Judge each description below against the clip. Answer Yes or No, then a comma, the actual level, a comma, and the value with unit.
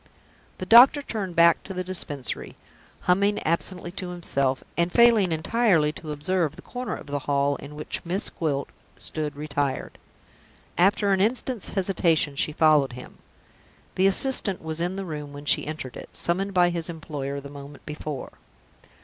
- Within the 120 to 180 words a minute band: Yes, average, 160 wpm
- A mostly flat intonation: No, average, 4.6 semitones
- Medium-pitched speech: Yes, medium, 170 Hz